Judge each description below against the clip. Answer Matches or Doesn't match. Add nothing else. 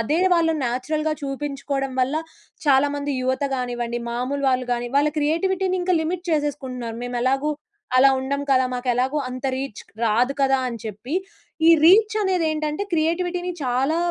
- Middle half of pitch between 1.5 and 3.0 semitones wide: Doesn't match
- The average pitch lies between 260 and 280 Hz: Matches